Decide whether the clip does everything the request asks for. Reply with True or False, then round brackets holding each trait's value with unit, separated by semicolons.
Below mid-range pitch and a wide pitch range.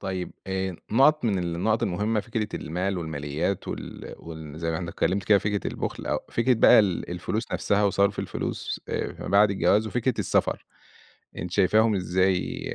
False (95 Hz; 3.5 semitones)